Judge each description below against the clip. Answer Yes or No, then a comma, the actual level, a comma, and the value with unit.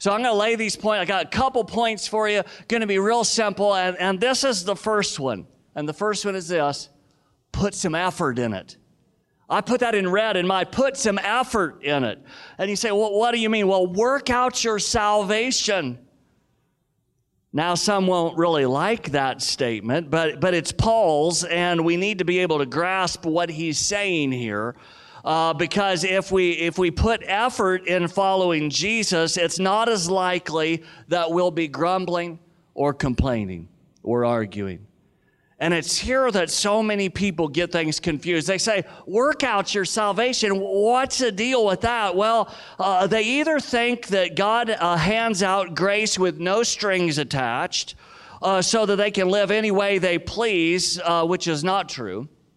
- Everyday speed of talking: Yes, average, 180 wpm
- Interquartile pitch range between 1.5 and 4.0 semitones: No, average, 4.4 semitones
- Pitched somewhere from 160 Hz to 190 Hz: Yes, medium, 185 Hz